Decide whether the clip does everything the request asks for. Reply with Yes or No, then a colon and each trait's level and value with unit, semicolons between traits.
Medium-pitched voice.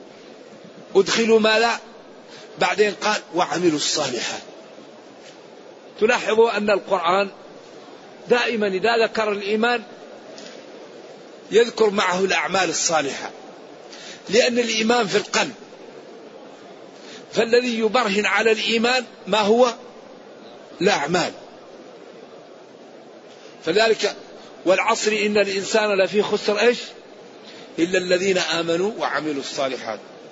No: high, 220 Hz